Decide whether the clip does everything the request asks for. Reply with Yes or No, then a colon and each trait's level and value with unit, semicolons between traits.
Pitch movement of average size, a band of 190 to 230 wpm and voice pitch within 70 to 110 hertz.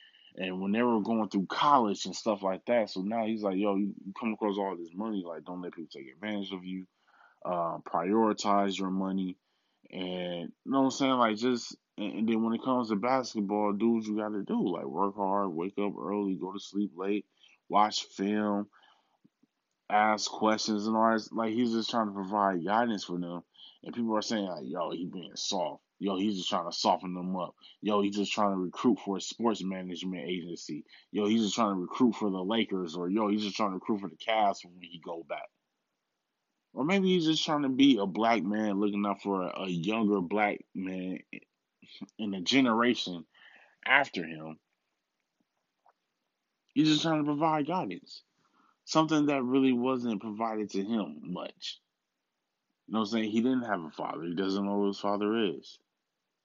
Yes: average, 3.1 semitones; average, 200 wpm; low, 105 Hz